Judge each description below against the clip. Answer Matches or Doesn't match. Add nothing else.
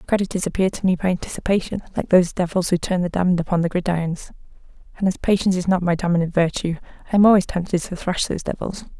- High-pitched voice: Doesn't match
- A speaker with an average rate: Doesn't match